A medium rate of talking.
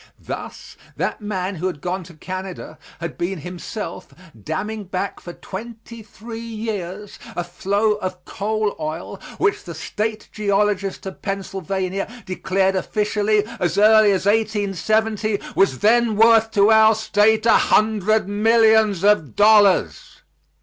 No: slow, 130 wpm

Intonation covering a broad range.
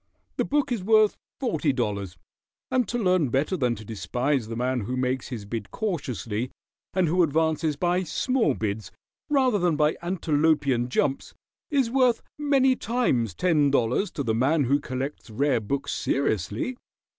Yes: wide, 7.5 semitones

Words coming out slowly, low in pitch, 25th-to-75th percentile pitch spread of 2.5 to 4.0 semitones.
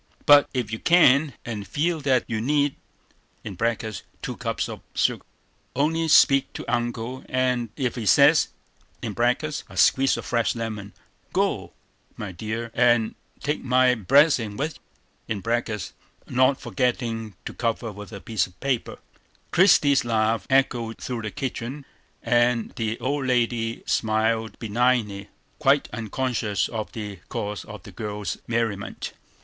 Yes: slow, 130 wpm; low, 120 Hz; average, 3.0 semitones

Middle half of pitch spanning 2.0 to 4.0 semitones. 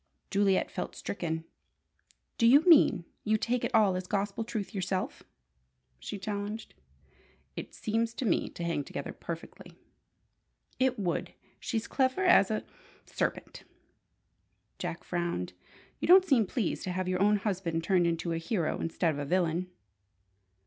No: average, 4.6 semitones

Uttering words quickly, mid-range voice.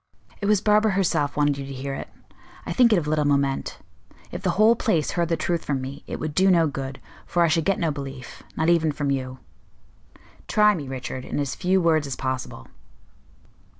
Yes: fast, 210 wpm; medium, 155 Hz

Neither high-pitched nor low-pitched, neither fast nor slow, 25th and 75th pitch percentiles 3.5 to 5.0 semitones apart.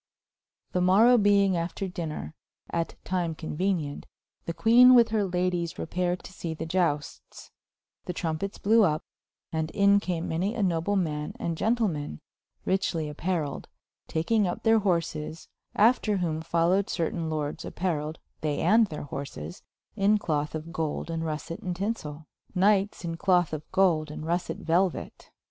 Yes: medium, 175 Hz; average, 150 wpm; average, 3.8 semitones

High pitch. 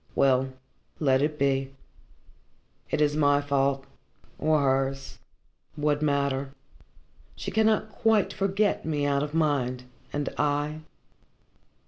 No: medium, 145 Hz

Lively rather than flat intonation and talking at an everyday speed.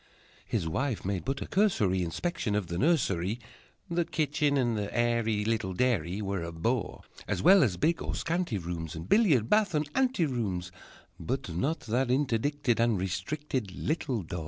Yes: wide, 7.7 semitones; average, 170 wpm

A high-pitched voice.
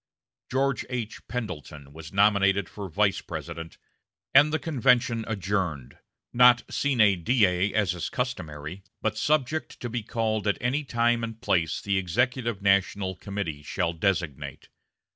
No: low, 100 Hz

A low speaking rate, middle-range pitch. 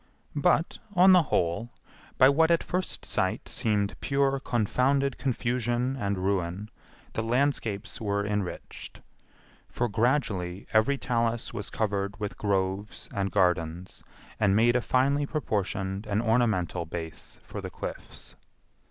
No: slow, 125 wpm; low, 110 Hz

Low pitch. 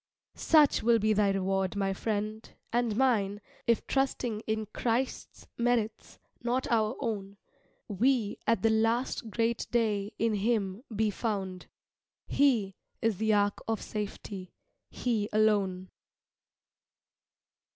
No: high, 215 Hz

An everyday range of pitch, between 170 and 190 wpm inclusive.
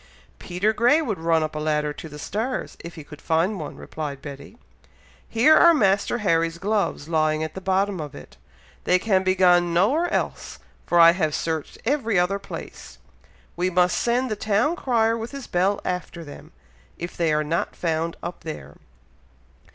Yes: average, 5.0 semitones; average, 180 wpm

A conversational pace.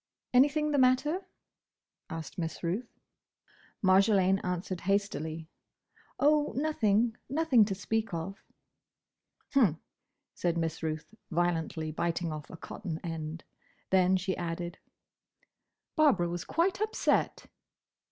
No: slow, 105 wpm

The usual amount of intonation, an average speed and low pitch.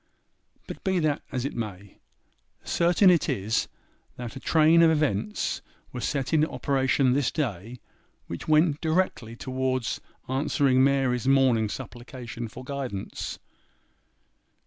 No: average, 4.0 semitones; slow, 125 wpm; low, 130 Hz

